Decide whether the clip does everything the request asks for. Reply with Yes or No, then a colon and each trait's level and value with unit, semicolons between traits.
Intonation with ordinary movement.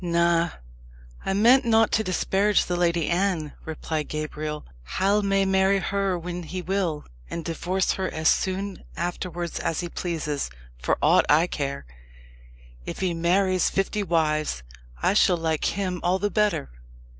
Yes: average, 3.1 semitones